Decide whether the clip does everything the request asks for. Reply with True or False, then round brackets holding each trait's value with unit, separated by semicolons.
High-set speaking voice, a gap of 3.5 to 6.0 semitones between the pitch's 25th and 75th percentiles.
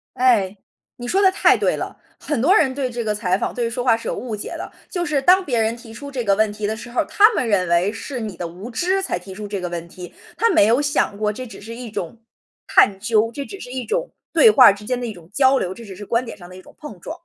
True (230 Hz; 4.7 semitones)